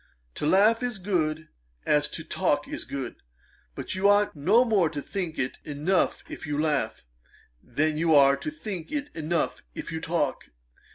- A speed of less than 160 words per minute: No, average, 170 wpm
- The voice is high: No, medium, 160 Hz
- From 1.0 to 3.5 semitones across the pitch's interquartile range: No, average, 4.6 semitones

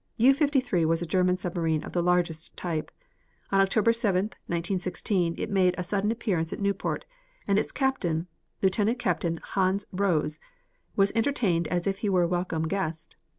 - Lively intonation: No, average, 2.9 semitones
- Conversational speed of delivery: Yes, average, 165 wpm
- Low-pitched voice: No, medium, 185 Hz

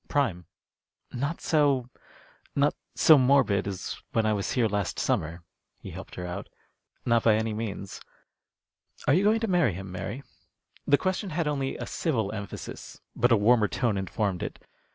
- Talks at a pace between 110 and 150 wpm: No, average, 170 wpm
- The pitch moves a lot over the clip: Yes, wide, 6.2 semitones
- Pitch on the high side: No, low, 115 Hz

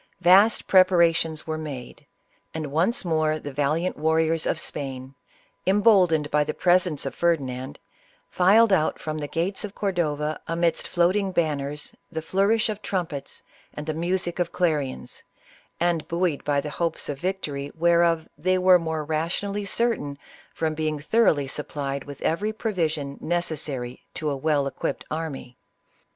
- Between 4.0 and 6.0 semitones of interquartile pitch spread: No, average, 3.6 semitones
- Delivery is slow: No, average, 145 wpm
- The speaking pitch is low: No, medium, 160 Hz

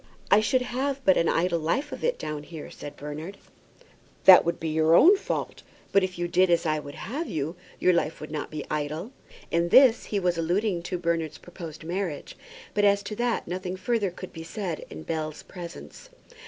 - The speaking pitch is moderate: Yes, medium, 175 Hz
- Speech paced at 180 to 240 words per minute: Yes, average, 200 wpm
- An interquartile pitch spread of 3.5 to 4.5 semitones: Yes, average, 4.1 semitones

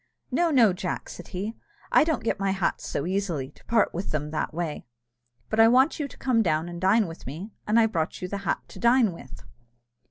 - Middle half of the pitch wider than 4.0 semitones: Yes, average, 5.2 semitones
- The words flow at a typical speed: No, fast, 225 wpm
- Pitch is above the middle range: Yes, high, 195 Hz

